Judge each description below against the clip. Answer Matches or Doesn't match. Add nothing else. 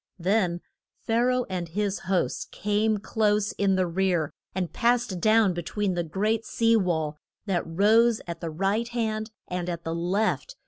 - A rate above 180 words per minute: Doesn't match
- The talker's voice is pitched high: Matches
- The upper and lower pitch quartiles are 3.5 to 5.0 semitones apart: Matches